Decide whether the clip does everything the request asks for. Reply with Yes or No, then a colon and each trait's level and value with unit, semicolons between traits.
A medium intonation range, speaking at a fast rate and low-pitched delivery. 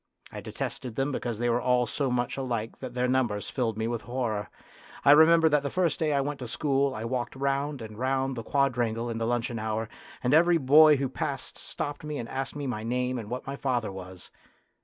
Yes: average, 3.2 semitones; fast, 220 wpm; low, 125 Hz